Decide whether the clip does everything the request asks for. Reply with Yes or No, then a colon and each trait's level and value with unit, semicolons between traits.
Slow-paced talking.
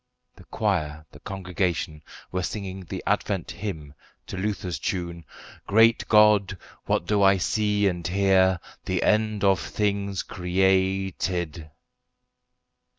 Yes: slow, 115 wpm